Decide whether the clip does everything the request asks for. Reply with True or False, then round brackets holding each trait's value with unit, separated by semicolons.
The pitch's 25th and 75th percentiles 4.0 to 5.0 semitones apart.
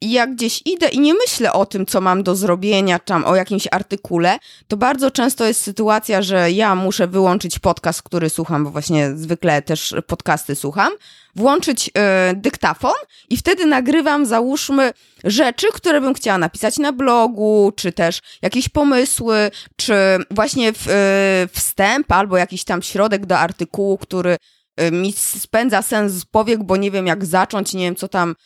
True (4.6 semitones)